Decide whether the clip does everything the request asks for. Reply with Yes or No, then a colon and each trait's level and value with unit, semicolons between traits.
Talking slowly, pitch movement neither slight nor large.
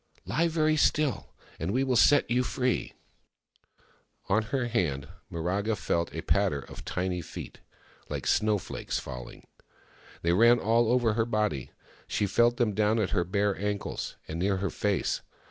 No: average, 160 wpm; average, 4.5 semitones